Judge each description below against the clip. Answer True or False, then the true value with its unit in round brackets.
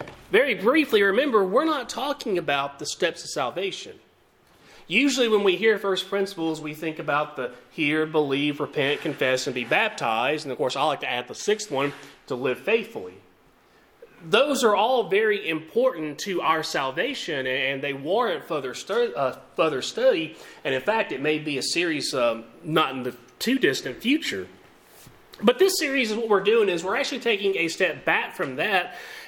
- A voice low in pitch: False (200 Hz)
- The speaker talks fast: False (180 wpm)